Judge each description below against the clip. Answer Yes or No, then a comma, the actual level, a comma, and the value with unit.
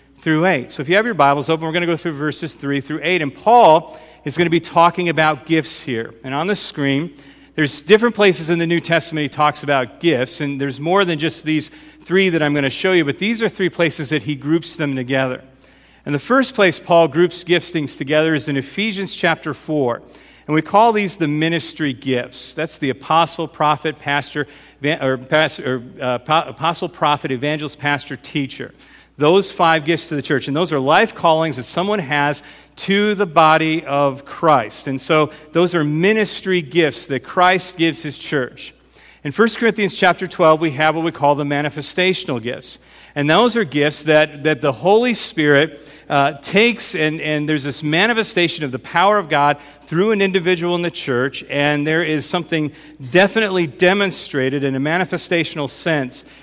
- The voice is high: No, medium, 155 Hz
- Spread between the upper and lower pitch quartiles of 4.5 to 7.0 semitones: No, average, 3.4 semitones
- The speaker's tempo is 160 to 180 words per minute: No, average, 190 wpm